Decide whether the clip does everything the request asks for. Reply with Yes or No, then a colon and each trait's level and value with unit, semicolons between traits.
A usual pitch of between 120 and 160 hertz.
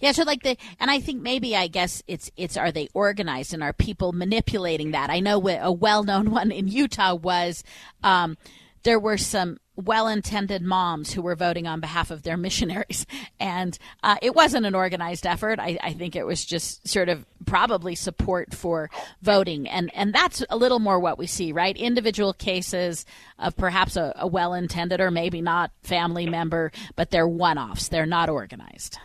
No: medium, 185 Hz